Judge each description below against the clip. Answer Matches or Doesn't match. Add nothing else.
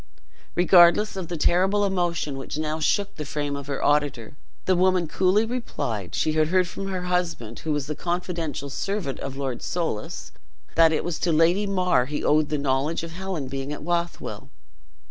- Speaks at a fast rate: Doesn't match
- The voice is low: Doesn't match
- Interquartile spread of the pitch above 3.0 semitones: Matches